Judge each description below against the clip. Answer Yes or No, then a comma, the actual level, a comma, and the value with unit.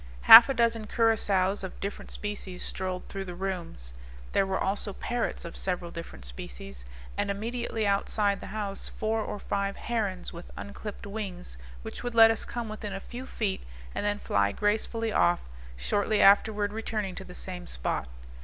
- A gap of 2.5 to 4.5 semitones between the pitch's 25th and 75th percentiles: Yes, average, 3.1 semitones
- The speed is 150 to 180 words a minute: Yes, average, 170 wpm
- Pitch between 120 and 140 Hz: No, high, 200 Hz